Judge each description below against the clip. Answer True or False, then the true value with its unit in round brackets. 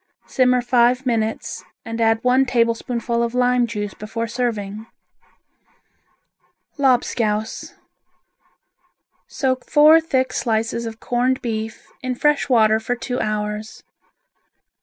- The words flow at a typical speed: False (105 wpm)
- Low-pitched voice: False (235 Hz)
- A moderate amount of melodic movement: False (2.2 semitones)